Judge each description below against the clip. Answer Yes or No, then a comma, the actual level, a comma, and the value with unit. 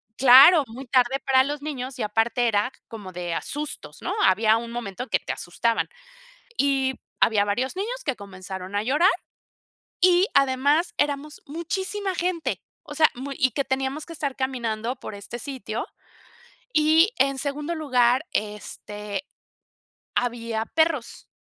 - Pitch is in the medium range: No, very high, 260 Hz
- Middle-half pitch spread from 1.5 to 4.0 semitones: No, average, 4.8 semitones